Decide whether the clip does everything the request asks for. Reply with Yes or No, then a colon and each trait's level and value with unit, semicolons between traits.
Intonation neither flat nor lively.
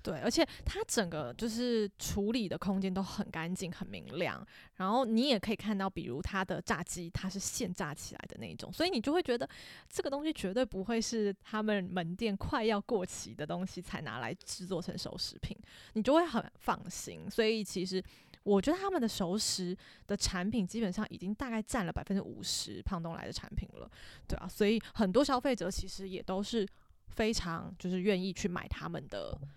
Yes: average, 3.8 semitones